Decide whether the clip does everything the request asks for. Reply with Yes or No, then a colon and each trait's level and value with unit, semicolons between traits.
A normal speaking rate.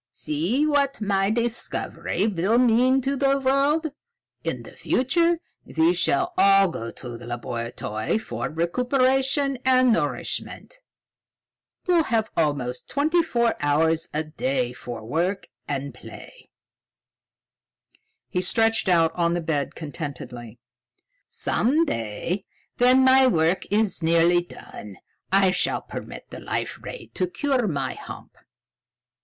No: slow, 125 wpm